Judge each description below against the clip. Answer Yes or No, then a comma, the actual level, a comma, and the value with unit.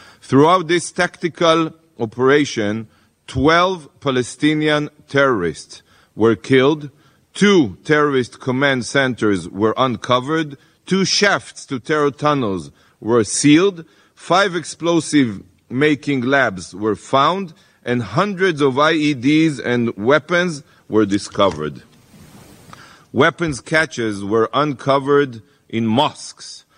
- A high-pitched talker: No, medium, 140 Hz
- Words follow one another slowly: Yes, slow, 95 wpm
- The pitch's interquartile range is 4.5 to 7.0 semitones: Yes, average, 5.3 semitones